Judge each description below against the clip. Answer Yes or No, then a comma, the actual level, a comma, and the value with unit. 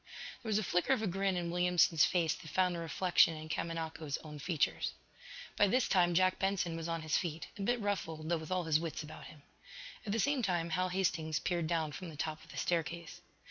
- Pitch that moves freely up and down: No, average, 2.7 semitones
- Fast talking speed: Yes, fast, 225 wpm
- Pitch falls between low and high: Yes, medium, 170 Hz